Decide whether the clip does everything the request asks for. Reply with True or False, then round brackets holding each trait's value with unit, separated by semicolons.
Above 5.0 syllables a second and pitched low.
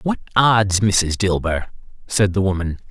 False (4.2 syllables/s; 100 Hz)